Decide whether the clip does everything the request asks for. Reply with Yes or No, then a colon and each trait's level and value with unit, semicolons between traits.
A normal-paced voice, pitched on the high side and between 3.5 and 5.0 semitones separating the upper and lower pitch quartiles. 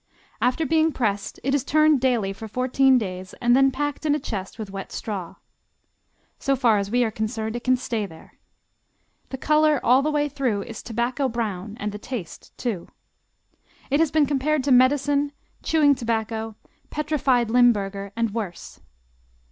Yes: average, 165 wpm; high, 245 Hz; average, 4.5 semitones